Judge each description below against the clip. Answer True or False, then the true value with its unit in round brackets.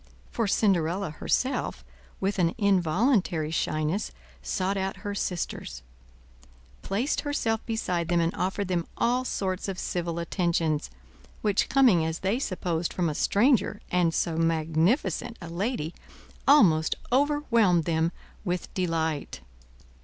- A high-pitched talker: False (180 Hz)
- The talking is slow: True (125 wpm)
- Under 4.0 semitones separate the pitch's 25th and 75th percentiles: False (4.3 semitones)